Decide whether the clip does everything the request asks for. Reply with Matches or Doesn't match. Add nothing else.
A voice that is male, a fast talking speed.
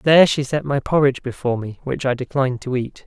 Matches